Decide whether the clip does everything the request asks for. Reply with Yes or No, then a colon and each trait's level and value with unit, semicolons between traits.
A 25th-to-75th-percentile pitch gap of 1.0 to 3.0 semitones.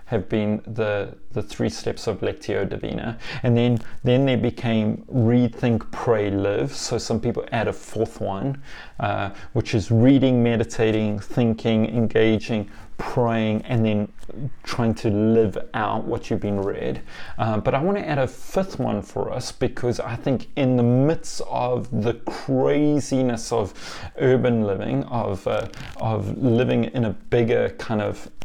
Yes: narrow, 2.6 semitones